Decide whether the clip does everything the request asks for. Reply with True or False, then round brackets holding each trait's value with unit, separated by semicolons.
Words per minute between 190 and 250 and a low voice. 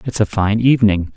True (205 wpm; 110 Hz)